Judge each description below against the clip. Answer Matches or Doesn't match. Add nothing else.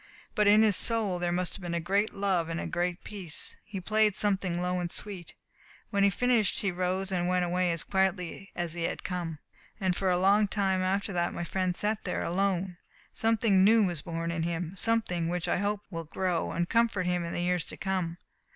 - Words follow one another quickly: Matches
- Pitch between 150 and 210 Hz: Matches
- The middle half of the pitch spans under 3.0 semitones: Matches